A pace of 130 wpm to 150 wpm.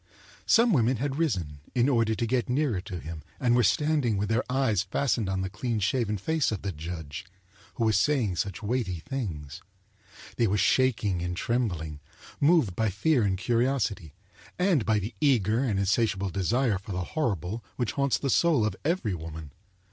No: average, 180 wpm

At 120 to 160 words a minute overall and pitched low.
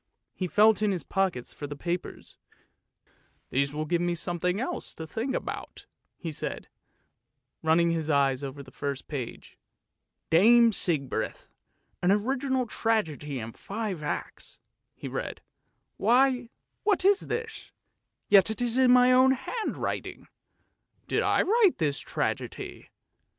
No: average, 145 wpm; high, 190 Hz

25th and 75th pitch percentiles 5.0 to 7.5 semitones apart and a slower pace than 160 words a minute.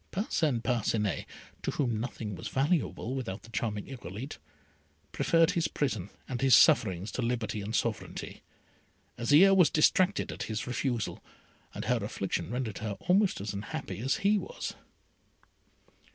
Yes: wide, 5.4 semitones; average, 140 wpm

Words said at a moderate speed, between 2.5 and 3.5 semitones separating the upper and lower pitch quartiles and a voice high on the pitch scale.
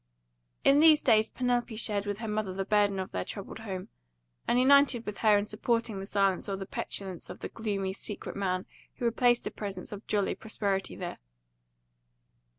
Yes: average, 180 wpm; average, 2.9 semitones; high, 210 Hz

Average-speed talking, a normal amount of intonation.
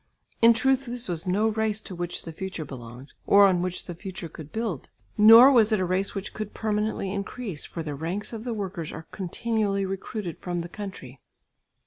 Yes: average, 195 wpm; average, 4.0 semitones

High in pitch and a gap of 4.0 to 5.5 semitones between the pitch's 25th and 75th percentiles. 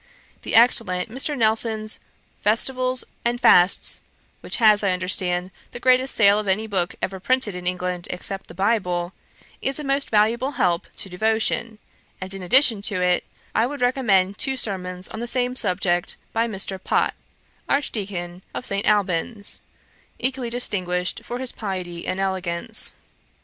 Yes: high, 205 Hz; average, 4.6 semitones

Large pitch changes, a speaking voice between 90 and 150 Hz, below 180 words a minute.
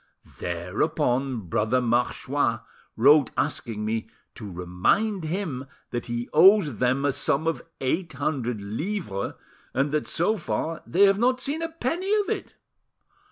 Yes: wide, 8.7 semitones; medium, 140 Hz; average, 140 wpm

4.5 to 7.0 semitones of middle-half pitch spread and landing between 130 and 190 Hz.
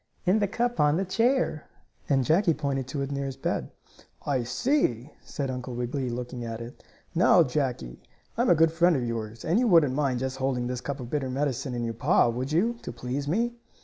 Yes: average, 4.8 semitones; low, 135 Hz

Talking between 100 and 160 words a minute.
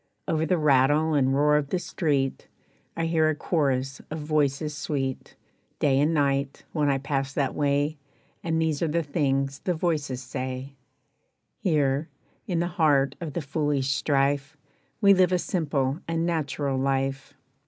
Yes: average, 155 wpm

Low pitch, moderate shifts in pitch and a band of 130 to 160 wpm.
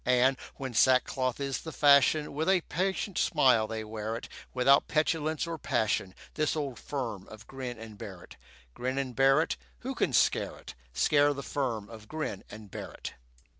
No: low, 130 Hz; average, 4.8 semitones; average, 170 wpm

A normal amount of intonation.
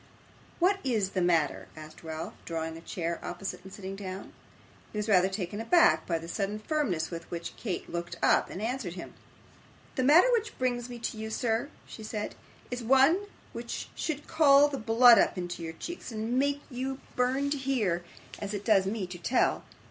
No: wide, 6.6 semitones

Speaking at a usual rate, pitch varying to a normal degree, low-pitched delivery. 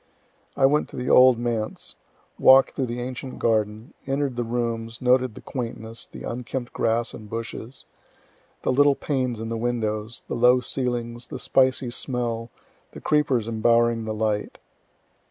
No: average, 155 wpm; narrow, 2.0 semitones; low, 120 Hz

